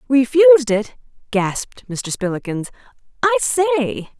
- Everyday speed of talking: No, slow, 100 wpm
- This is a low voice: No, high, 230 Hz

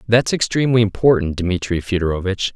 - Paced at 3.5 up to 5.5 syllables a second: No, 5.9 syllables/s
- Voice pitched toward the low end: Yes, low, 105 Hz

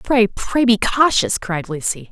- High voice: Yes, high, 220 Hz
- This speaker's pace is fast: No, average, 170 wpm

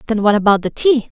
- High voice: Yes, high, 225 Hz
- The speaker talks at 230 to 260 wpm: Yes, fast, 250 wpm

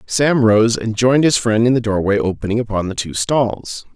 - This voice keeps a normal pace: No, fast, 210 wpm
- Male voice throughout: Yes, male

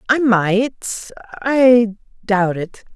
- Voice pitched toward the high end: Yes, high, 220 Hz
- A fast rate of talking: No, slow, 60 wpm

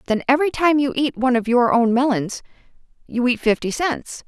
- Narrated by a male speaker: No, female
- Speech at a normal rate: Yes, average, 195 wpm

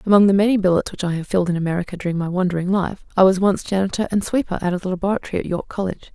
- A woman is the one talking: Yes, female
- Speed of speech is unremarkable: No, fast, 265 wpm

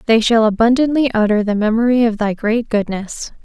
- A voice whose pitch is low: No, high, 225 Hz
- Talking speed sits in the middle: Yes, average, 175 wpm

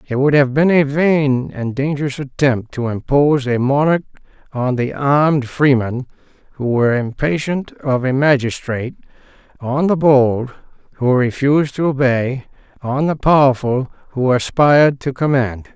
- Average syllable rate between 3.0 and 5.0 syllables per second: Yes, 4.6 syllables/s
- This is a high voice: No, low, 135 Hz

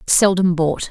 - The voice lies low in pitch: No, medium, 175 Hz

